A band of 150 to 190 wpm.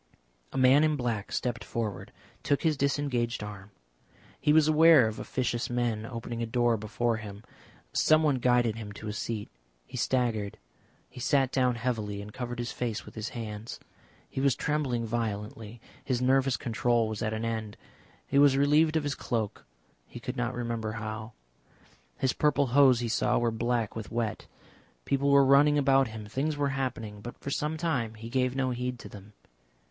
Yes: average, 180 wpm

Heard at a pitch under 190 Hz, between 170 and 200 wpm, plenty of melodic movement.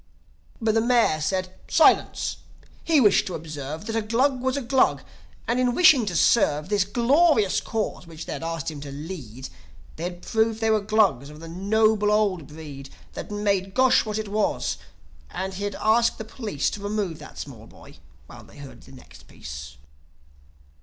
No: high, 205 Hz; average, 180 wpm; wide, 5.8 semitones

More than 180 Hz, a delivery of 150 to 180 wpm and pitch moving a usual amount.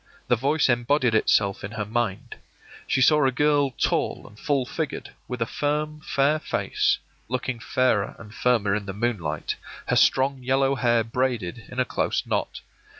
No: low, 125 Hz; average, 165 wpm; average, 3.5 semitones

